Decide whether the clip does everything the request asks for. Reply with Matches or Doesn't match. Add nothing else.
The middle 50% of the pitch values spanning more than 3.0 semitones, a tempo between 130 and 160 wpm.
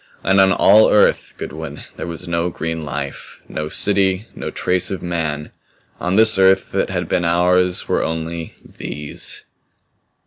Doesn't match